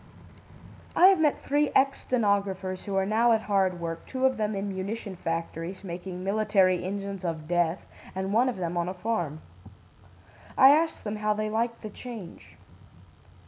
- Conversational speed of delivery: Yes, average, 170 wpm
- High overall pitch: Yes, high, 200 Hz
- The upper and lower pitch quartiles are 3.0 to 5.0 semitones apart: Yes, average, 3.7 semitones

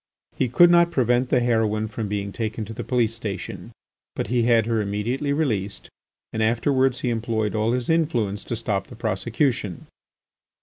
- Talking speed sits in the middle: Yes, average, 170 wpm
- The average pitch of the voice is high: No, low, 115 Hz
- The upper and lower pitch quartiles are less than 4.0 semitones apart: Yes, average, 2.8 semitones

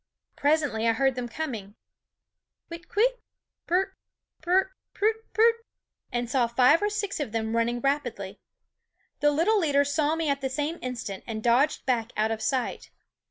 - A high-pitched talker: Yes, very high, 275 Hz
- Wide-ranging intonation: Yes, wide, 5.8 semitones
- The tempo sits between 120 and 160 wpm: No, average, 175 wpm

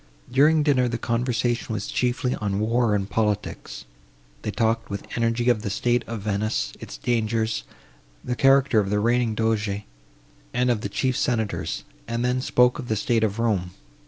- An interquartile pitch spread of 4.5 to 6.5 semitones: No, average, 2.7 semitones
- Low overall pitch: Yes, low, 115 Hz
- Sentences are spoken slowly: No, average, 170 wpm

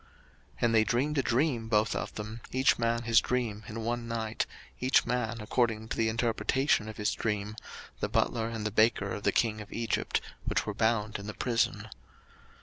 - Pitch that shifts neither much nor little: No, narrow, 1.7 semitones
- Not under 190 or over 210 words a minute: Yes, average, 195 wpm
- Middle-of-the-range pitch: No, low, 115 Hz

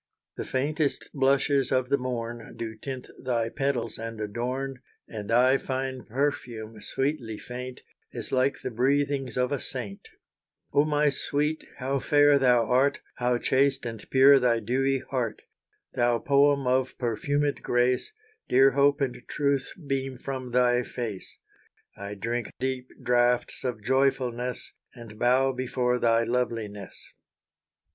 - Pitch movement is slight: Yes, narrow, 2.3 semitones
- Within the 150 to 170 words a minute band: No, slow, 135 wpm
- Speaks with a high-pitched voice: No, low, 125 Hz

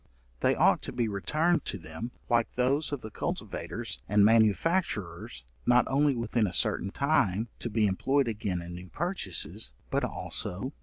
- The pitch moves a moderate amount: No, wide, 6.2 semitones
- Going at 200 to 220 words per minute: No, average, 165 wpm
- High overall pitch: No, low, 115 Hz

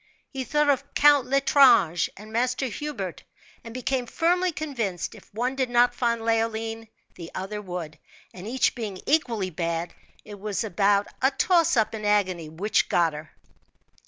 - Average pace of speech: Yes, average, 160 wpm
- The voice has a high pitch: Yes, high, 225 Hz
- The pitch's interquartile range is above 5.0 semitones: Yes, wide, 5.5 semitones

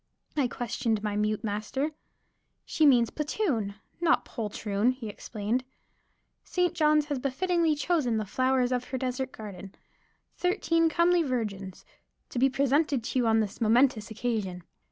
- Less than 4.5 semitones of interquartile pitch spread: No, wide, 5.4 semitones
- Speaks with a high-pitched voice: Yes, very high, 250 Hz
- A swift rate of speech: No, average, 140 wpm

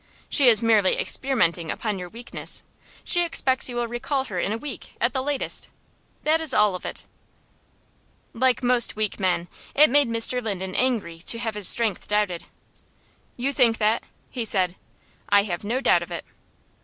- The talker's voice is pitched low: No, high, 230 Hz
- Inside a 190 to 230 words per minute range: No, average, 175 wpm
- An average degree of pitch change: Yes, average, 4.2 semitones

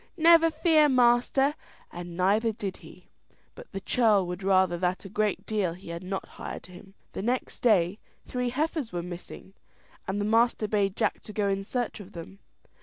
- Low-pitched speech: No, high, 205 Hz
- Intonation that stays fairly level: No, average, 4.7 semitones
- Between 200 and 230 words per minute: No, average, 180 wpm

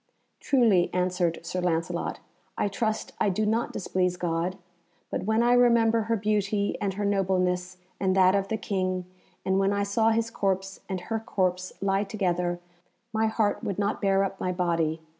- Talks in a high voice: Yes, high, 195 Hz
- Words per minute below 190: Yes, average, 175 wpm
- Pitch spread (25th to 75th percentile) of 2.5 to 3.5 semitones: Yes, average, 2.9 semitones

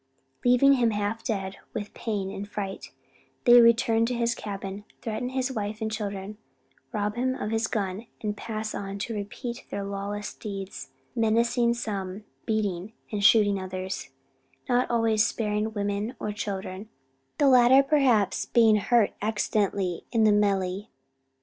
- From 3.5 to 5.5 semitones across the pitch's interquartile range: No, narrow, 2.6 semitones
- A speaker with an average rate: Yes, average, 145 wpm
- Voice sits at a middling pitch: No, high, 215 Hz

